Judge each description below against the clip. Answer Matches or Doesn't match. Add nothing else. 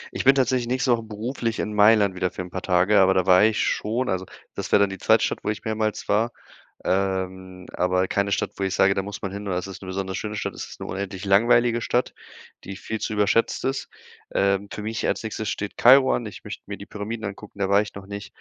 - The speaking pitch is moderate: Doesn't match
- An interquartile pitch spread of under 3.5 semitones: Matches